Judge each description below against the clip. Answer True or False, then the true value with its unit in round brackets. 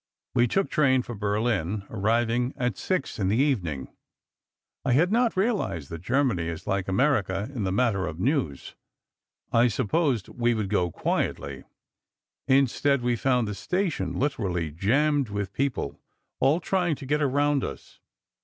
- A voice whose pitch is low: True (120 Hz)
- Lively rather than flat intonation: True (6.3 semitones)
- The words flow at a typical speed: True (155 wpm)